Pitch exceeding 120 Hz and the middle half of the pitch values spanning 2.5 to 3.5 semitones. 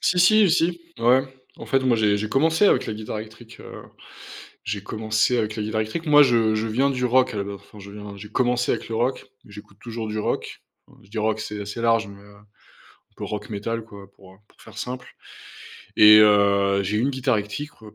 No: low, 110 Hz; average, 3.2 semitones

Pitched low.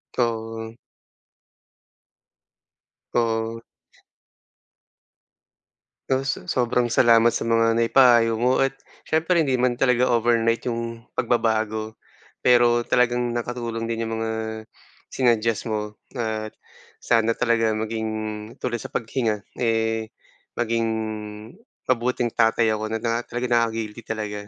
Yes: low, 115 Hz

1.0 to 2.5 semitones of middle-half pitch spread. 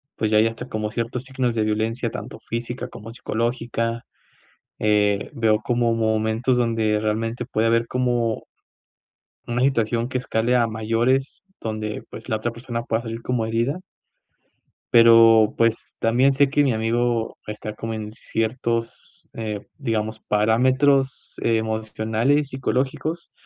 Yes: narrow, 1.9 semitones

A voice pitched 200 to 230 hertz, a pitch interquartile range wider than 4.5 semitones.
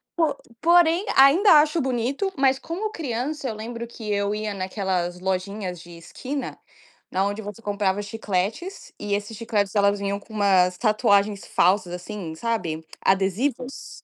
Yes: high, 210 Hz; average, 5.2 semitones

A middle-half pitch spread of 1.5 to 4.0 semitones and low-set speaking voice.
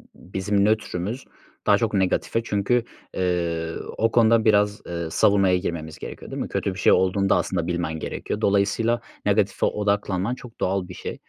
Yes: average, 3.1 semitones; low, 100 Hz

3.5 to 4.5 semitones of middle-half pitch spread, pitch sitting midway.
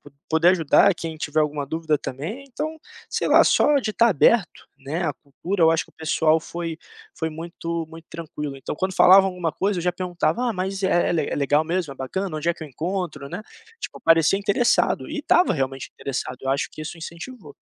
Yes: average, 3.8 semitones; medium, 165 Hz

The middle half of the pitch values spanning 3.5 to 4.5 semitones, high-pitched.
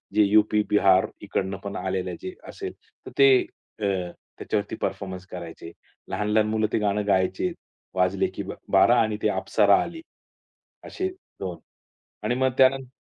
No: average, 4.1 semitones; low, 105 Hz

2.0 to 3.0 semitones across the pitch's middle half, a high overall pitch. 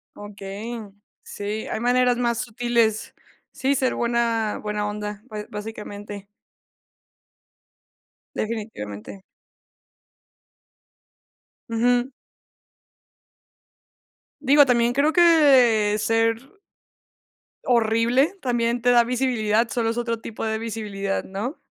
Yes: average, 2.7 semitones; high, 230 Hz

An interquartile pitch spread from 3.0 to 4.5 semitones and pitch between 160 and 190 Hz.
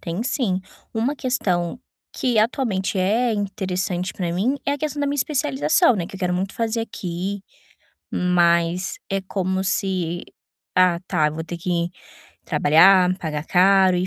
Yes: average, 3.7 semitones; medium, 185 Hz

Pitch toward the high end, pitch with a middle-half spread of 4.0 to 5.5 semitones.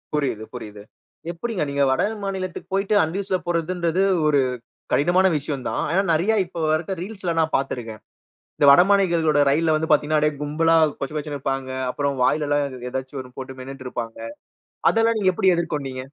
No: medium, 155 Hz; average, 4.6 semitones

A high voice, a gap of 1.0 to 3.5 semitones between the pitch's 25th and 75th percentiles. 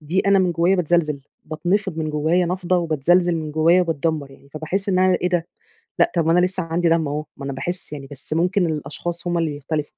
No: medium, 165 Hz; average, 2.7 semitones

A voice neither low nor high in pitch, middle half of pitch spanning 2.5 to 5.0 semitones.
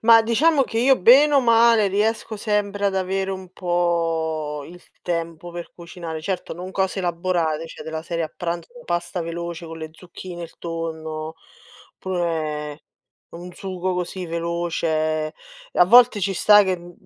Yes: medium, 175 Hz; average, 2.8 semitones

